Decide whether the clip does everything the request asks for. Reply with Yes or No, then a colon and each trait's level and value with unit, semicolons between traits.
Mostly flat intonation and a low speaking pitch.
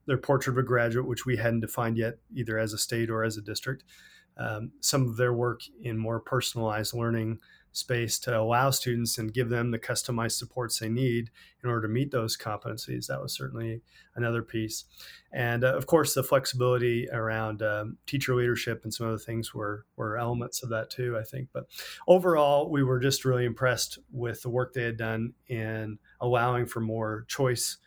Yes: narrow, 2.1 semitones; low, 120 Hz